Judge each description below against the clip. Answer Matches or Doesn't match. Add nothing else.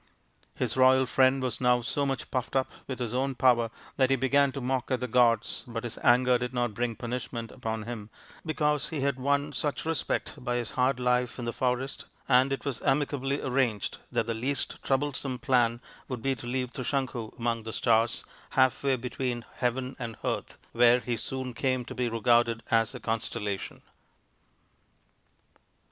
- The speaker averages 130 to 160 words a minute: Doesn't match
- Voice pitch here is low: Matches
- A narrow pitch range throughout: Matches